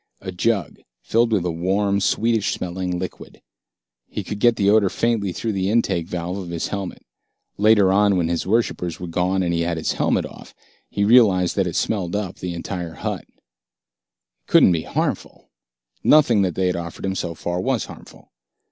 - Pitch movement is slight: No, average, 3.0 semitones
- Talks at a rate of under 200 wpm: Yes, average, 185 wpm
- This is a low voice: Yes, very low, 95 Hz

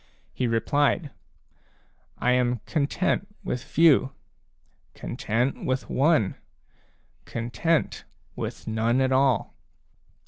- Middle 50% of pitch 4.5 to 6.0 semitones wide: No, average, 3.4 semitones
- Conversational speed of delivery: No, slow, 95 wpm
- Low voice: Yes, low, 130 Hz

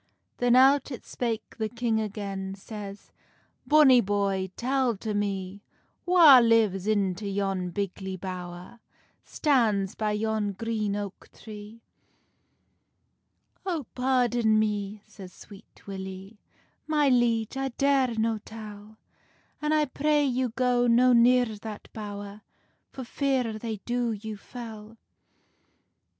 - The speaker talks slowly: Yes, slow, 120 wpm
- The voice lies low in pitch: No, high, 220 Hz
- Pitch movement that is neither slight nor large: Yes, average, 3.5 semitones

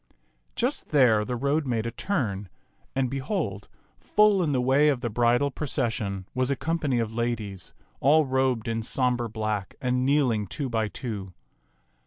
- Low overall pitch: Yes, low, 125 Hz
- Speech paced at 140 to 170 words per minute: Yes, average, 160 wpm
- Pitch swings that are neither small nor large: Yes, average, 3.8 semitones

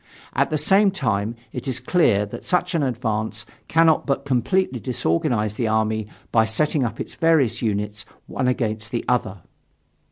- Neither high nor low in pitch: No, low, 120 Hz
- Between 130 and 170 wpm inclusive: Yes, average, 160 wpm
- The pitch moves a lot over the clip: Yes, wide, 5.7 semitones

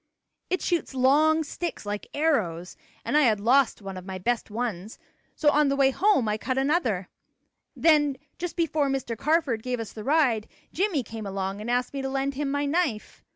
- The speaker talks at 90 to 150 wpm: No, average, 195 wpm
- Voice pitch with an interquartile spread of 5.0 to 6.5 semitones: Yes, wide, 5.5 semitones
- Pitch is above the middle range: Yes, very high, 265 Hz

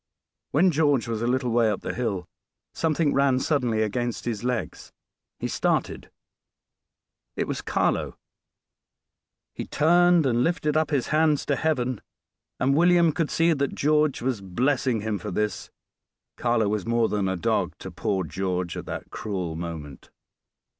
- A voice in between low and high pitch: No, low, 125 Hz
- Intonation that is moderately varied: No, wide, 6.1 semitones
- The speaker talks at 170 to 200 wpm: No, average, 155 wpm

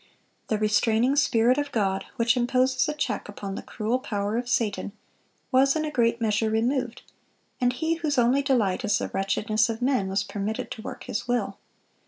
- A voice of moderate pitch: No, high, 235 Hz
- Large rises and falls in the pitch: No, average, 3.3 semitones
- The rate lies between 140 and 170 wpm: No, average, 185 wpm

